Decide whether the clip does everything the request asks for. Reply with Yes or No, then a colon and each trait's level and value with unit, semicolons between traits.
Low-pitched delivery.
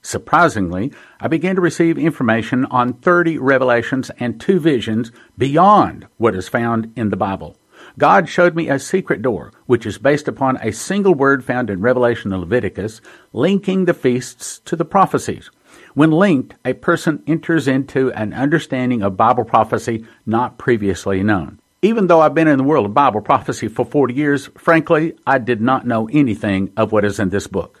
Yes: low, 125 Hz